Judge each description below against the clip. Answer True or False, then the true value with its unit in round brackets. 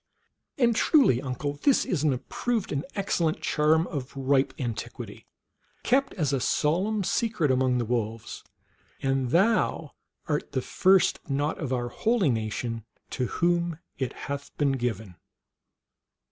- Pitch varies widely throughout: True (6.1 semitones)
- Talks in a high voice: False (145 Hz)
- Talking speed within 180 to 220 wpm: False (135 wpm)